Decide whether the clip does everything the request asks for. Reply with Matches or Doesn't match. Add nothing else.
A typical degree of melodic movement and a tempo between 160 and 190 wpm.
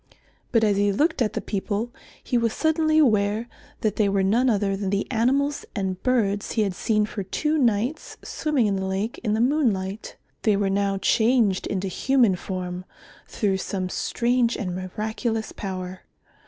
Matches